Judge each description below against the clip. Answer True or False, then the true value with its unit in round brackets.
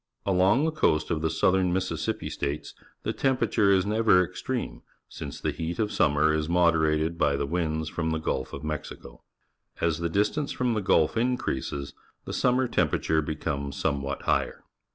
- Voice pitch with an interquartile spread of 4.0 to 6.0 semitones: True (4.6 semitones)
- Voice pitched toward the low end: True (85 Hz)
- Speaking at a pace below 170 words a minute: True (155 wpm)